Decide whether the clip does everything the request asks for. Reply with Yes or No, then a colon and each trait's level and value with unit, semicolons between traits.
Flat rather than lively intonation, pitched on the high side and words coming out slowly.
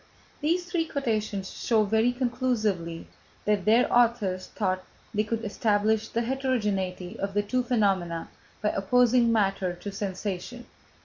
No: average, 3.9 semitones; high, 215 Hz; slow, 130 wpm